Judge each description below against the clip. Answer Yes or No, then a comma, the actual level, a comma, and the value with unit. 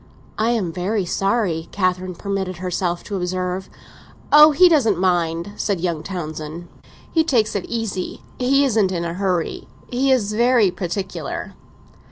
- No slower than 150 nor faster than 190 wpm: No, average, 140 wpm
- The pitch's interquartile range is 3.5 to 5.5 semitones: Yes, average, 4.2 semitones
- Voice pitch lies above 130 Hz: Yes, high, 190 Hz